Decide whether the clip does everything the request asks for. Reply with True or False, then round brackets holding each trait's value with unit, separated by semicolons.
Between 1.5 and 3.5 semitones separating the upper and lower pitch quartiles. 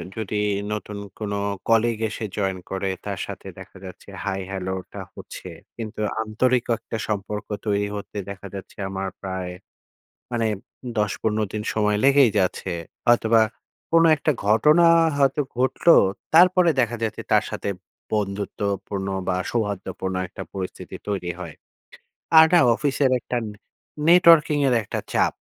False (4.2 semitones)